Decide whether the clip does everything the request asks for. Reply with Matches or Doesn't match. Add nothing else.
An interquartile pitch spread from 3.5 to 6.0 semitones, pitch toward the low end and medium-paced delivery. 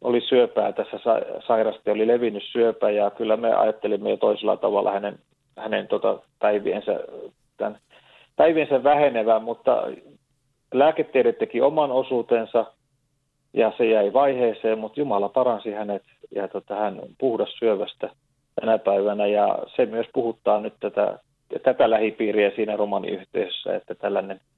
Matches